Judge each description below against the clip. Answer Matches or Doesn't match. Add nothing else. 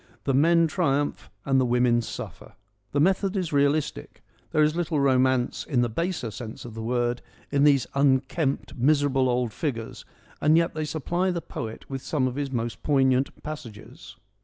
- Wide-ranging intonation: Doesn't match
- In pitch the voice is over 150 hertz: Doesn't match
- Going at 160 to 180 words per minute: Matches